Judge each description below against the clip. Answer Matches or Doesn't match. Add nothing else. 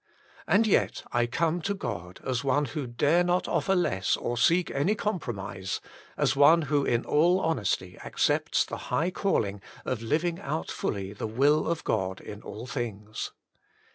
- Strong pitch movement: Matches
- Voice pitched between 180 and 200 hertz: Doesn't match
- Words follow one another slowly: Doesn't match